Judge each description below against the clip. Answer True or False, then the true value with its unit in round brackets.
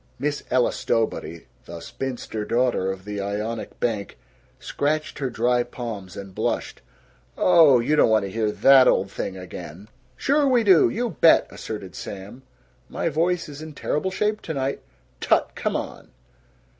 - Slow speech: False (155 wpm)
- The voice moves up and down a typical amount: False (7.1 semitones)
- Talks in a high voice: False (120 Hz)